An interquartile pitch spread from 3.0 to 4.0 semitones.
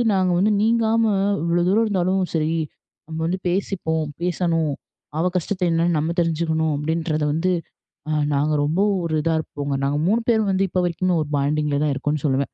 Yes: average, 3.4 semitones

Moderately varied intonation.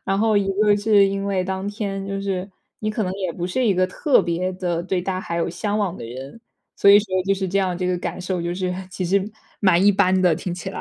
No: narrow, 1.7 semitones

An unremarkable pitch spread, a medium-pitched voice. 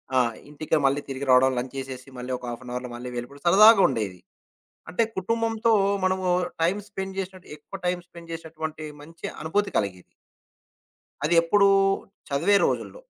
No: wide, 6.5 semitones; medium, 160 Hz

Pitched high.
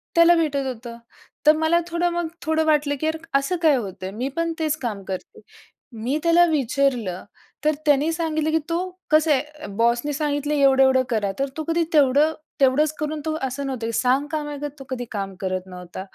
Yes: very high, 290 Hz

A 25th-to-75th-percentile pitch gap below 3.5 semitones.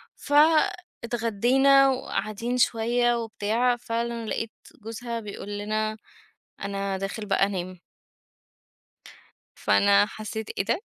Yes: average, 2.8 semitones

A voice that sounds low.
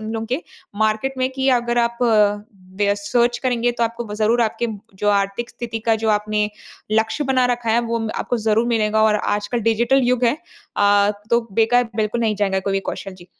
No: high, 225 Hz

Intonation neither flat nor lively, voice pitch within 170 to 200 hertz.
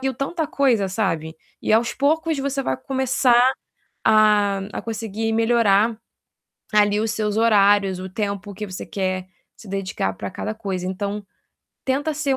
No: average, 3.8 semitones; high, 215 Hz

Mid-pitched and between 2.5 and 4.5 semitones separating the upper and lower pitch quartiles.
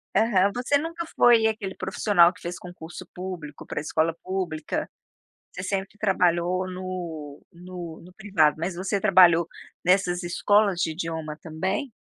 Yes: medium, 180 Hz; average, 2.8 semitones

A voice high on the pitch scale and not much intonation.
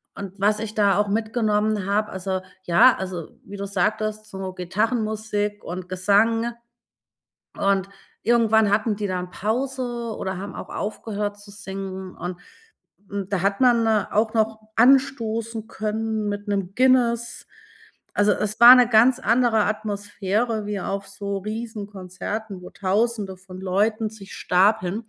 Yes: high, 210 Hz; narrow, 2.2 semitones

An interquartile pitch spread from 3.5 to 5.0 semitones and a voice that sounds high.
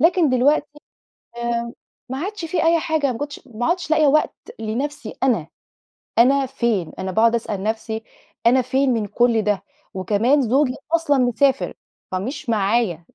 Yes: average, 4.7 semitones; very high, 250 Hz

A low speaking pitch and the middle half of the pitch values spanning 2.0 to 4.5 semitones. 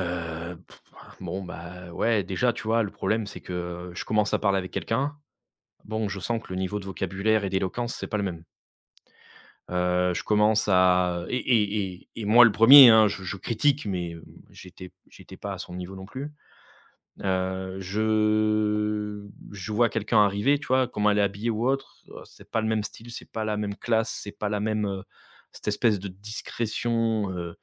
Yes: low, 105 Hz; average, 2.9 semitones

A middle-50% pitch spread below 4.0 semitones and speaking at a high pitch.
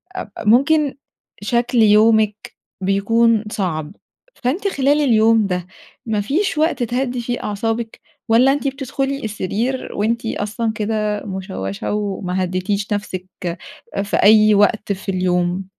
Yes: average, 3.5 semitones; high, 215 Hz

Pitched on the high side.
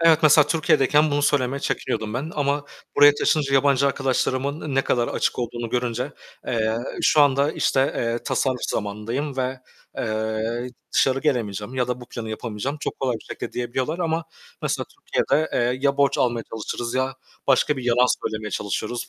No: low, 130 Hz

